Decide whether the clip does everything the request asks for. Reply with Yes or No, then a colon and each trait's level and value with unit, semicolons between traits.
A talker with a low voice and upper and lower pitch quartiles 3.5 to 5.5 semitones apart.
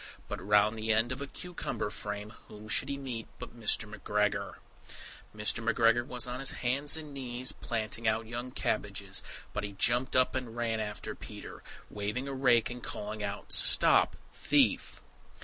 No: low, 115 Hz; average, 3.0 semitones